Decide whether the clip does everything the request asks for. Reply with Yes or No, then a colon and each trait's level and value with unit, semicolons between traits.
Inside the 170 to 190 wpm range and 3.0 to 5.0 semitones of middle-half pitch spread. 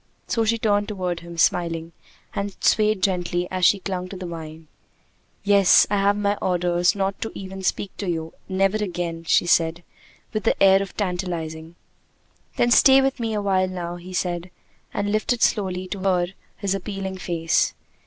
No: average, 175 wpm; narrow, 2.5 semitones